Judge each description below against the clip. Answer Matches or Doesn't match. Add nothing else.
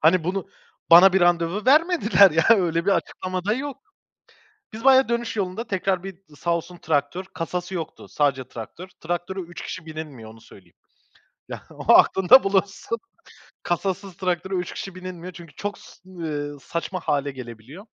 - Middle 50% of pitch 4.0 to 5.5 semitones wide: Doesn't match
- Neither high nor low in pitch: Matches